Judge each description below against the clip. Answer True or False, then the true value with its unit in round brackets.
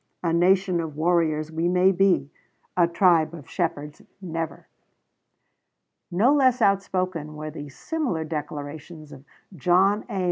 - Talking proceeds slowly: True (130 wpm)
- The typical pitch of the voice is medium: True (170 Hz)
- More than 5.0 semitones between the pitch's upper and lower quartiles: False (3.4 semitones)